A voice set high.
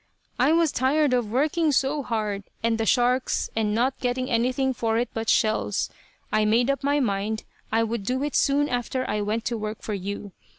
Yes: high, 240 Hz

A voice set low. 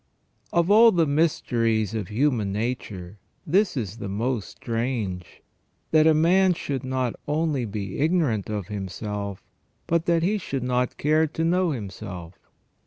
Yes: low, 125 Hz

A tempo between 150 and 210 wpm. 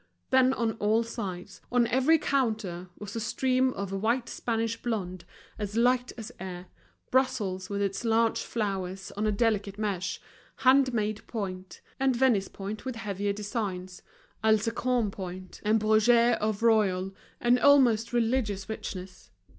No: average, 140 wpm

